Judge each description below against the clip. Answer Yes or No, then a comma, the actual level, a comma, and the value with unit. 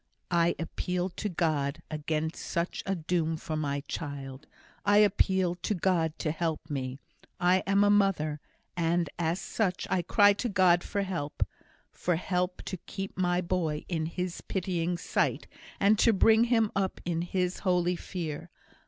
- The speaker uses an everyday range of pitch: Yes, average, 3.0 semitones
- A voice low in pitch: No, medium, 175 Hz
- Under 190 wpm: Yes, average, 160 wpm